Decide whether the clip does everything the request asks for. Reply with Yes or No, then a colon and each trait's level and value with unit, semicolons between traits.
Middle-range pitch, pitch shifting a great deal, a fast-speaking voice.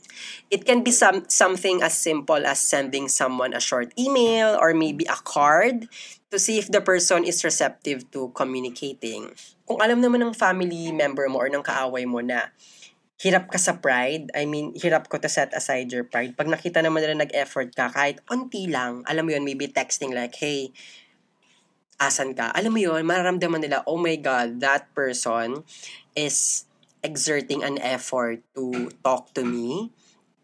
Yes: medium, 150 Hz; wide, 5.8 semitones; fast, 170 wpm